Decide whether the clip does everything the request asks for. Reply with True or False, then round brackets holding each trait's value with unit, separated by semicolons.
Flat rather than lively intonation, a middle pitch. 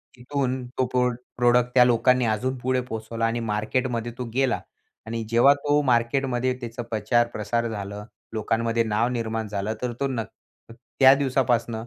False (2.1 semitones; 120 Hz)